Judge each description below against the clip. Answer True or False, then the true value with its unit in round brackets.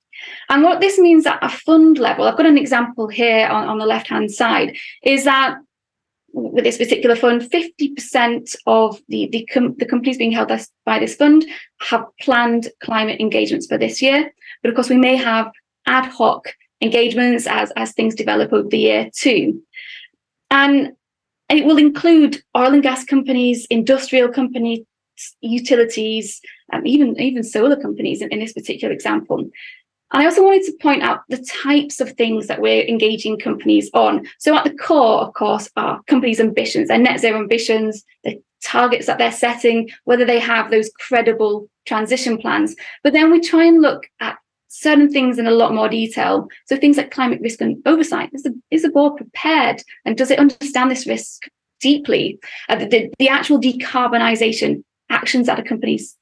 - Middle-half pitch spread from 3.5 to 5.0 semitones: True (4.0 semitones)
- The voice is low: False (255 Hz)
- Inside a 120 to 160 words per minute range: False (175 wpm)